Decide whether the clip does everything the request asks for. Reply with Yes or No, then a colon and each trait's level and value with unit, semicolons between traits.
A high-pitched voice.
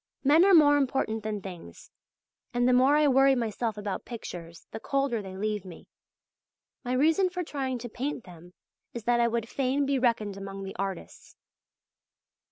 Yes: high, 240 Hz